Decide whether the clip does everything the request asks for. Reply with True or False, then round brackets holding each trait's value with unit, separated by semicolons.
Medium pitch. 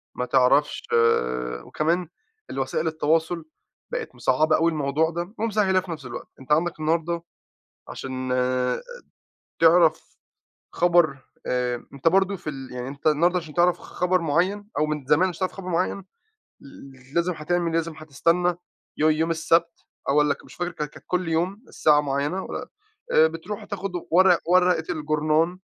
True (165 Hz)